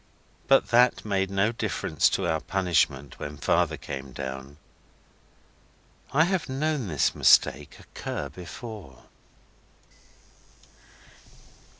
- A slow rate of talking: Yes, slow, 95 wpm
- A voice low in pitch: Yes, very low, 95 Hz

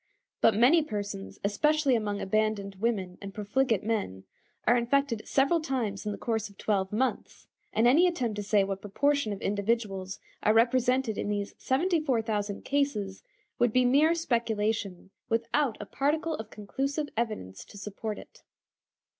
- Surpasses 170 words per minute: No, average, 150 wpm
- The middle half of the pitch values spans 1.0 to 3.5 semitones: No, average, 4.7 semitones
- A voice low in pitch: No, high, 225 Hz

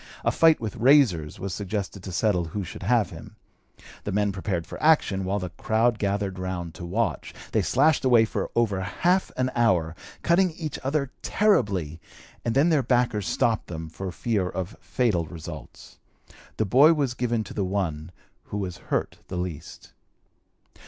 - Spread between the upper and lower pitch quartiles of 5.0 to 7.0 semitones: Yes, wide, 5.5 semitones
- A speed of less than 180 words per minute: Yes, average, 170 wpm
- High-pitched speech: No, low, 105 Hz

